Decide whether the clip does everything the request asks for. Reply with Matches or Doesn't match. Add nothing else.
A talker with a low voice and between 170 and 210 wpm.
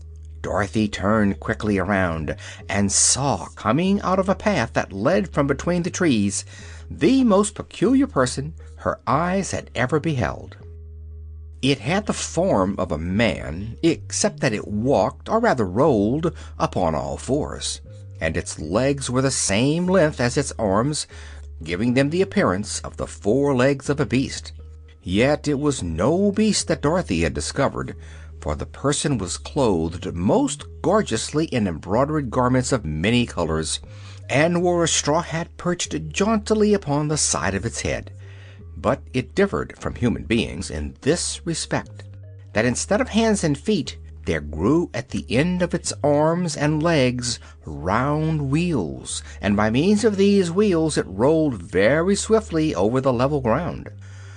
Doesn't match